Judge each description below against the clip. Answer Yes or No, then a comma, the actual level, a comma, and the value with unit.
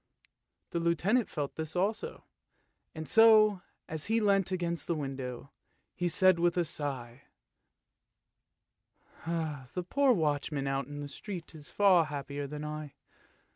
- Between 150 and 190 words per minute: No, slow, 135 wpm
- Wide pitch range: No, average, 4.4 semitones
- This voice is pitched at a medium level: Yes, medium, 160 Hz